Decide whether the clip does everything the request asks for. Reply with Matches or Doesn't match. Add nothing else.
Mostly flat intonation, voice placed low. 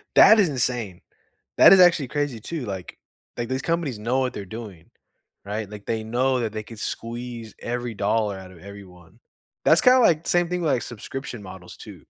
Doesn't match